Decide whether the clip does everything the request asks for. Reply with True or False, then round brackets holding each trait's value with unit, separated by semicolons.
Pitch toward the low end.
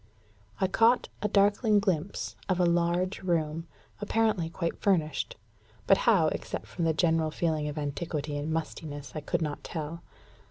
False (165 Hz)